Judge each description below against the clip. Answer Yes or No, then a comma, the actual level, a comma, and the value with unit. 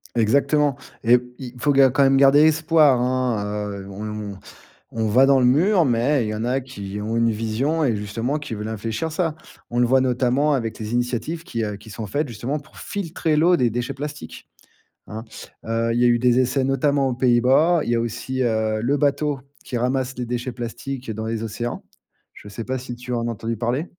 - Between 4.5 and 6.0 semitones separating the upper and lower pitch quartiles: No, average, 3.4 semitones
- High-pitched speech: No, low, 125 Hz